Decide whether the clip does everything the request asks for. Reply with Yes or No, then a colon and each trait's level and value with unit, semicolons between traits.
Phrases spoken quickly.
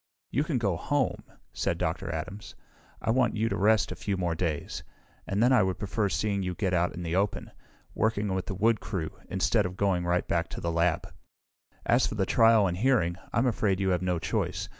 Yes: fast, 215 wpm